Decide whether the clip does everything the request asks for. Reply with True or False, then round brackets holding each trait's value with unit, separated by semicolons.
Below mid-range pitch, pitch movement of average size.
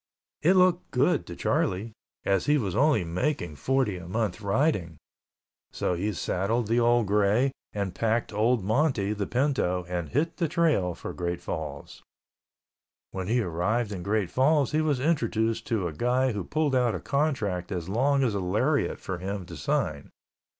False (110 Hz; 6.3 semitones)